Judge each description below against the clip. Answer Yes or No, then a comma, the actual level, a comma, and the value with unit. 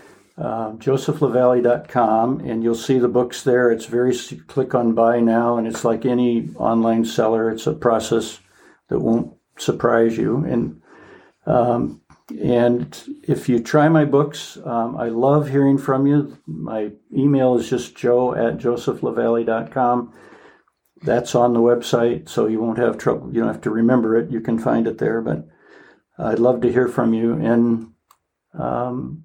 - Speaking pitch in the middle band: No, low, 120 Hz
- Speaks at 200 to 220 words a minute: No, average, 160 wpm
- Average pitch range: No, narrow, 1.8 semitones